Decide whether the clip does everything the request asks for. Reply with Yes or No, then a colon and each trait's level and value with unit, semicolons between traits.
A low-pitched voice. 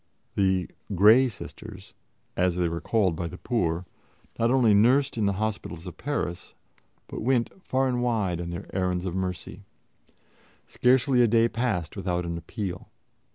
Yes: low, 100 Hz